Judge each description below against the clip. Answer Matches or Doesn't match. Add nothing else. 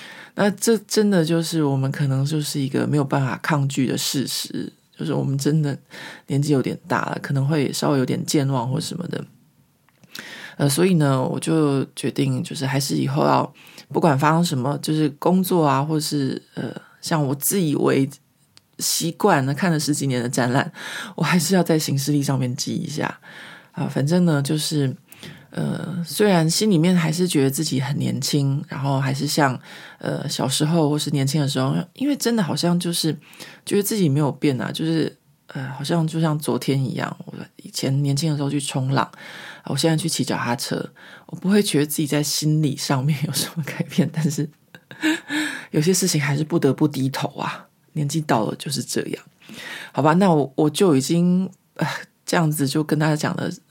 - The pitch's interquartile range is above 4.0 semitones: Doesn't match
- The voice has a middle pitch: Matches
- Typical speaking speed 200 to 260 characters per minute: Doesn't match